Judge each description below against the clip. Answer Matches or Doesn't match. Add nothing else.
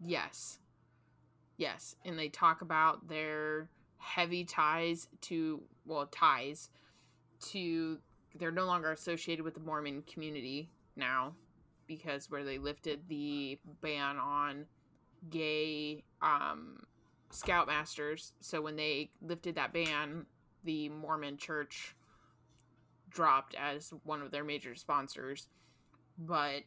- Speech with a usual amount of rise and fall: Doesn't match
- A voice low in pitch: Doesn't match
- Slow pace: Matches